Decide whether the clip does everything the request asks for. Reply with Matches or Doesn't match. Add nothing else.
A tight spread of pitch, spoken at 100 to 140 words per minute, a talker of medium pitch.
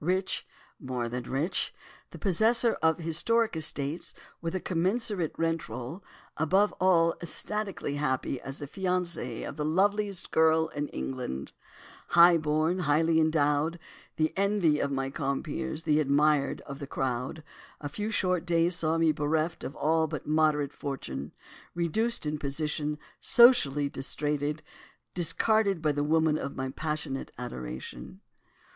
Doesn't match